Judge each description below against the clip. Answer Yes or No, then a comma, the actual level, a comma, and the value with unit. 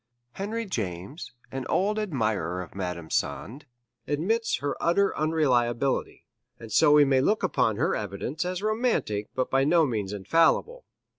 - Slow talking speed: No, average, 145 wpm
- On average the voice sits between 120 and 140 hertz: Yes, low, 135 Hz